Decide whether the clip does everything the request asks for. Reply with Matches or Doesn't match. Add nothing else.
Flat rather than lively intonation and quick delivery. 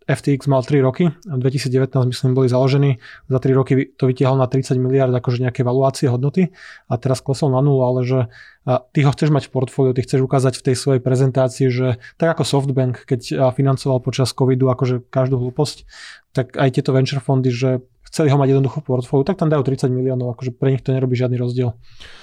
Matches